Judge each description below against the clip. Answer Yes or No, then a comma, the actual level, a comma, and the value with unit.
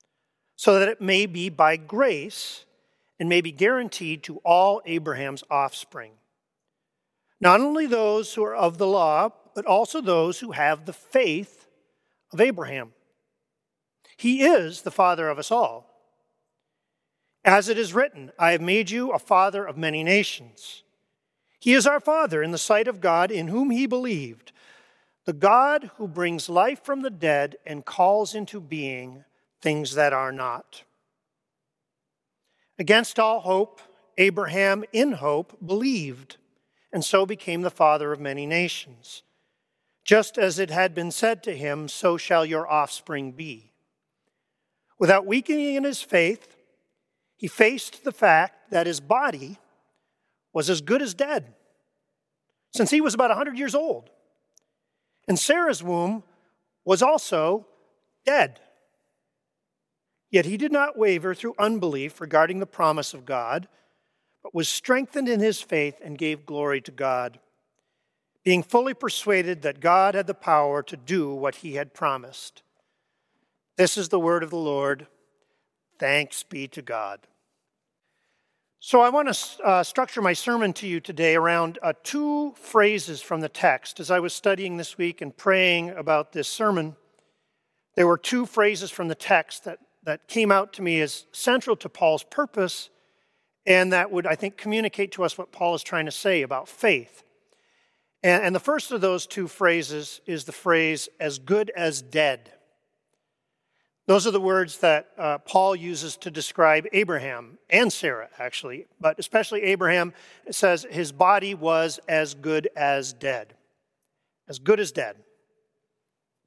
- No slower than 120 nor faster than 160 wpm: Yes, average, 150 wpm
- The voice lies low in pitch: No, medium, 185 Hz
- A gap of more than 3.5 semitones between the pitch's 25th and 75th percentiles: Yes, wide, 5.4 semitones